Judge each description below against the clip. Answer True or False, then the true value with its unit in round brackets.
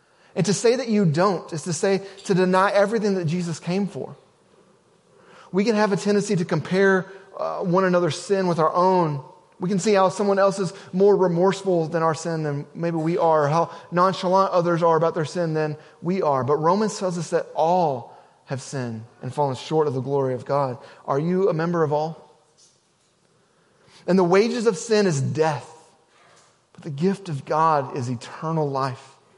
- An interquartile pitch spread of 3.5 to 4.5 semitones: True (4.0 semitones)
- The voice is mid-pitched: True (175 Hz)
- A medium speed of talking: True (190 wpm)